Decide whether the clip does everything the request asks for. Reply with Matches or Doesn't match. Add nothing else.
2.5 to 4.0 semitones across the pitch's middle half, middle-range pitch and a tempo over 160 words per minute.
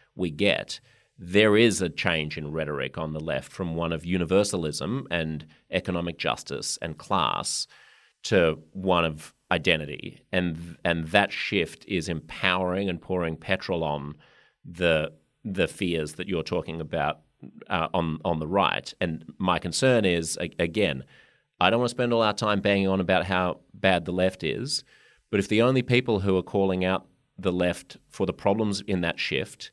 Doesn't match